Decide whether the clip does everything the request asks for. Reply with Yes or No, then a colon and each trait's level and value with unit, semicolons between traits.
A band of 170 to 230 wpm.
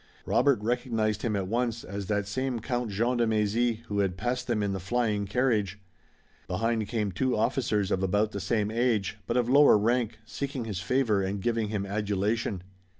Yes: average, 185 wpm